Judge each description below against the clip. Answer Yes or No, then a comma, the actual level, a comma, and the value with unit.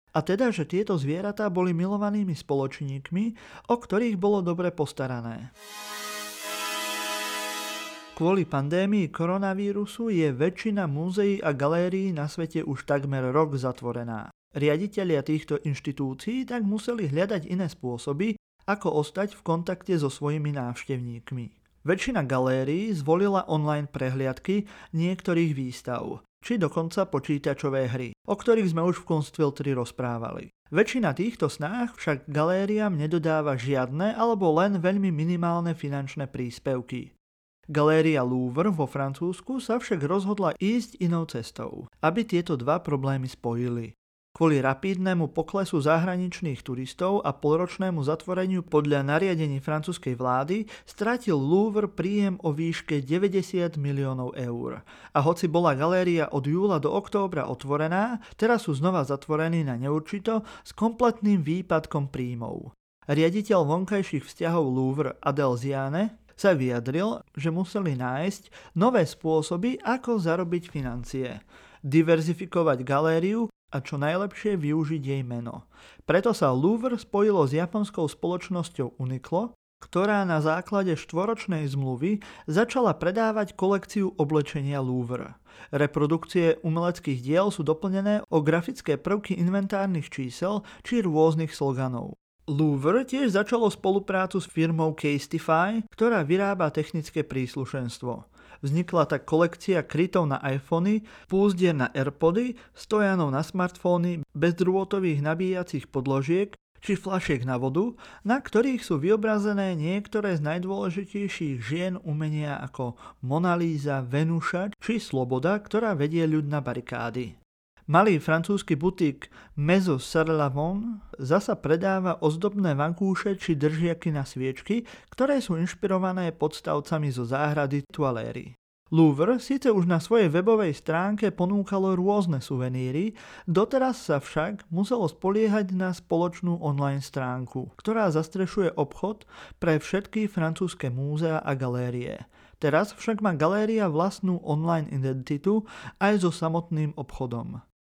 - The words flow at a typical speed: Yes, average, 120 wpm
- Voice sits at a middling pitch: Yes, medium, 165 Hz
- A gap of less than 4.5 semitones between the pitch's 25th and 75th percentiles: No, wide, 5.4 semitones